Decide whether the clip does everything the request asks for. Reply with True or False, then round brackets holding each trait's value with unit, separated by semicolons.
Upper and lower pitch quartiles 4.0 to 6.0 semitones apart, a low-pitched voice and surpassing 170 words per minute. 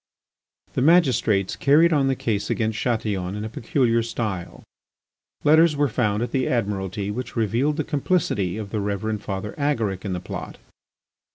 False (5.2 semitones; 115 Hz; 160 wpm)